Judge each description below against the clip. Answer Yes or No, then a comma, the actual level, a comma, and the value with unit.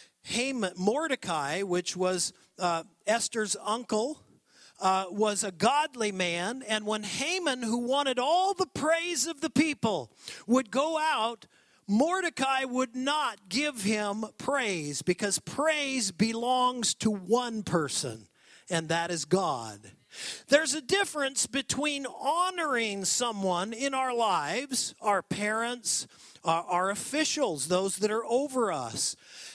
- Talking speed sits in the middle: No, slow, 125 wpm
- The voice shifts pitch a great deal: Yes, wide, 6.1 semitones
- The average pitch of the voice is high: Yes, high, 230 Hz